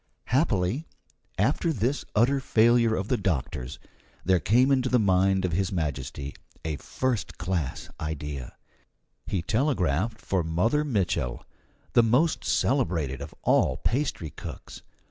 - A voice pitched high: No, very low, 95 Hz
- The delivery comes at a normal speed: No, slow, 125 wpm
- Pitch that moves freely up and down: Yes, wide, 7.6 semitones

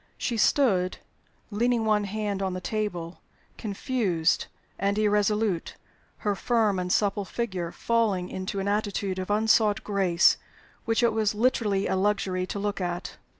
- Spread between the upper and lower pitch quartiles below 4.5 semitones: Yes, narrow, 2.6 semitones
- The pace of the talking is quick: No, average, 145 wpm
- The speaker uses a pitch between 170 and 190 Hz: No, high, 205 Hz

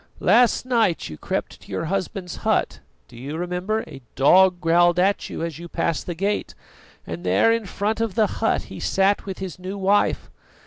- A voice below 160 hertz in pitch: No, medium, 185 Hz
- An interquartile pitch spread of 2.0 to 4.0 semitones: Yes, average, 3.4 semitones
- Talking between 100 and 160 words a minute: No, average, 190 wpm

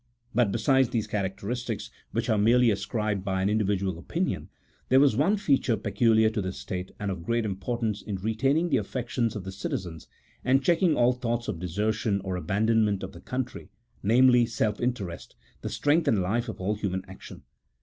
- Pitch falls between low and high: No, low, 110 Hz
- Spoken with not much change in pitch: No, average, 4.0 semitones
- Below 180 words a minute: No, average, 185 wpm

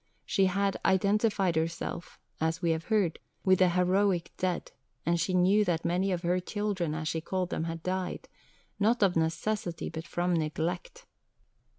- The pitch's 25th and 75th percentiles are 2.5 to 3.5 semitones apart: Yes, average, 2.9 semitones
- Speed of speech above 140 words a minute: Yes, average, 165 wpm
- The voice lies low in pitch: No, medium, 180 Hz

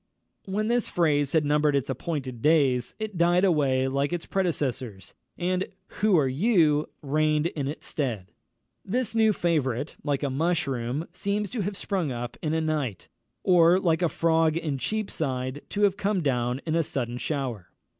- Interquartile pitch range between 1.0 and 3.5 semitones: No, average, 5.0 semitones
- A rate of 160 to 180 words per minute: Yes, average, 165 wpm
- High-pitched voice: No, medium, 155 Hz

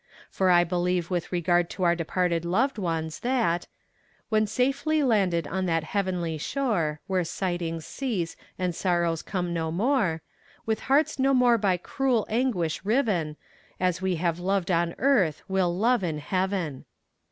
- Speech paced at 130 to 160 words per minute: Yes, average, 155 wpm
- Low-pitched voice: No, medium, 180 Hz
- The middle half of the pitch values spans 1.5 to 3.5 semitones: No, average, 4.4 semitones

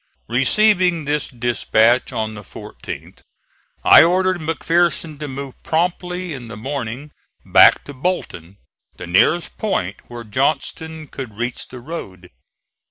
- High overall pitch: No, medium, 140 Hz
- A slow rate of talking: Yes, slow, 125 wpm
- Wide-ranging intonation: Yes, wide, 6.3 semitones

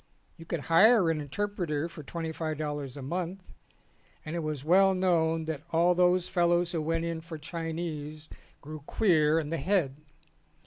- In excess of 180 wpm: No, average, 170 wpm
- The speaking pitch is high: No, medium, 165 Hz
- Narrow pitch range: Yes, narrow, 2.3 semitones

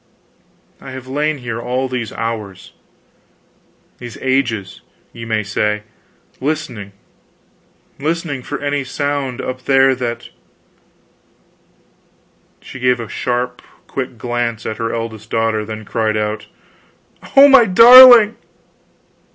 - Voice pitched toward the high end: No, low, 125 Hz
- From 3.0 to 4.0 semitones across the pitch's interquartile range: Yes, average, 3.6 semitones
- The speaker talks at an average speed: No, slow, 115 wpm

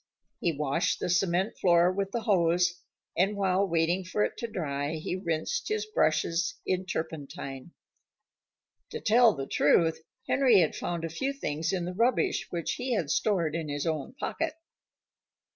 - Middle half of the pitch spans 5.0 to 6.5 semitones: No, average, 4.3 semitones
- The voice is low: No, medium, 175 Hz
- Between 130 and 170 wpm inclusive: Yes, average, 160 wpm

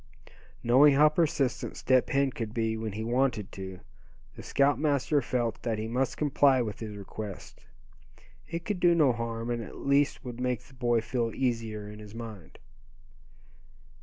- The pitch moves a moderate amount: Yes, average, 3.7 semitones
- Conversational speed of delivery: Yes, average, 165 wpm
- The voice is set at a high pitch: No, low, 120 Hz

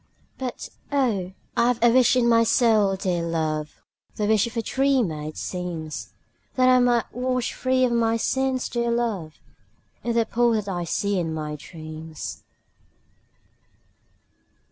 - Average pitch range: No, wide, 6.2 semitones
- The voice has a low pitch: No, high, 225 Hz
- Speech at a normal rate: Yes, average, 150 wpm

